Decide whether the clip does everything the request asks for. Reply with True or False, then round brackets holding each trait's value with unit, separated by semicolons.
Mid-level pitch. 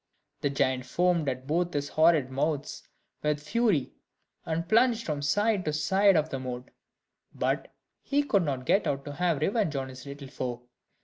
True (150 Hz)